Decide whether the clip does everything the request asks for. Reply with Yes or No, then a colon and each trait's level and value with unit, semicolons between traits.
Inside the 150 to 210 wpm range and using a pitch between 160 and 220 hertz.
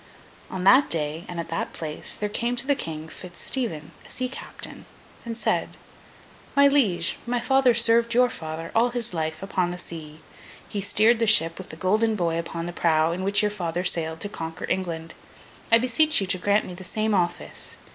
Yes: average, 200 wpm; medium, 185 Hz